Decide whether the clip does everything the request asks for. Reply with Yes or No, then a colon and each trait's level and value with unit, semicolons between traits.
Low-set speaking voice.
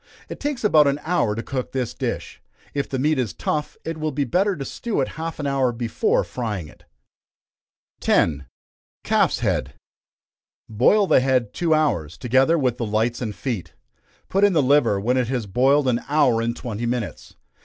Yes: low, 130 Hz